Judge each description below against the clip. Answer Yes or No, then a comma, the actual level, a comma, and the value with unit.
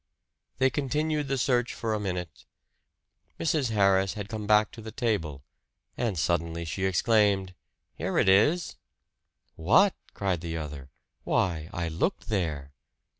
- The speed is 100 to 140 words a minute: Yes, slow, 135 wpm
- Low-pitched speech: Yes, low, 100 Hz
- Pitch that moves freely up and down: Yes, wide, 5.8 semitones